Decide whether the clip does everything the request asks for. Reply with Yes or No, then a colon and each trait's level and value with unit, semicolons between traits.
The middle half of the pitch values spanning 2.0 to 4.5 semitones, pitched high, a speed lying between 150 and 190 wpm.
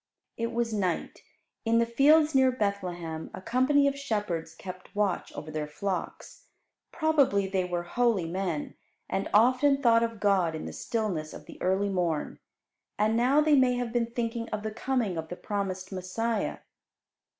No: average, 4.9 semitones; high, 215 Hz; average, 165 wpm